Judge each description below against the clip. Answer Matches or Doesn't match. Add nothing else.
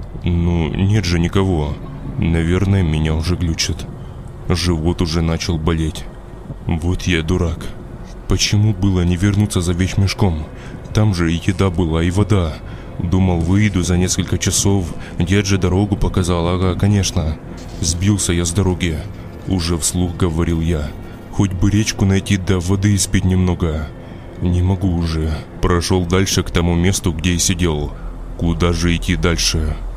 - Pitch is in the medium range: Doesn't match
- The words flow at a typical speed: Matches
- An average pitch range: Doesn't match